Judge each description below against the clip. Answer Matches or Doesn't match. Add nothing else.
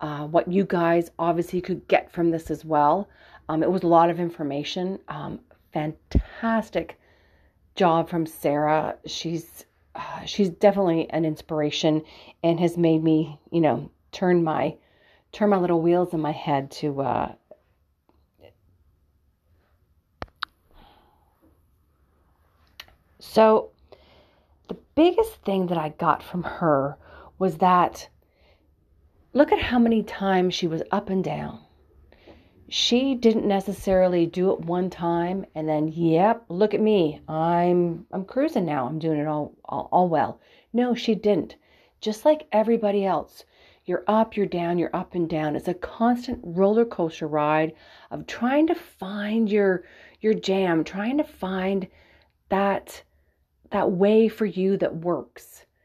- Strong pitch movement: Doesn't match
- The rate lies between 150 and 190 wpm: Doesn't match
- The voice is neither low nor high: Matches